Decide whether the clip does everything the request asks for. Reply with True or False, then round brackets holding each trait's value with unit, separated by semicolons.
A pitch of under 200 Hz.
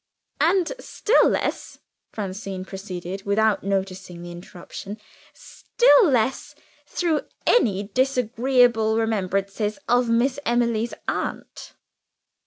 False (220 Hz)